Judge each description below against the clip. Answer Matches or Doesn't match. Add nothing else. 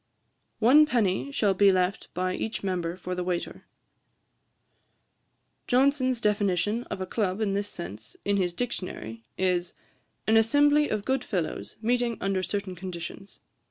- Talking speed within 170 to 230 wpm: Doesn't match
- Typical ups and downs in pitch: Matches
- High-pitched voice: Matches